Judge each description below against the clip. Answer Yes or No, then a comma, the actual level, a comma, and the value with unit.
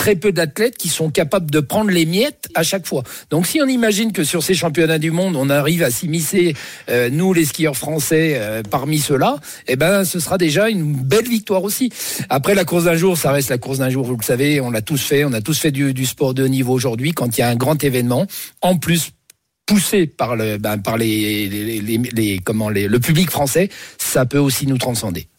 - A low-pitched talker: No, medium, 155 Hz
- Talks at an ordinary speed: No, fast, 240 wpm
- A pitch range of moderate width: No, wide, 5.7 semitones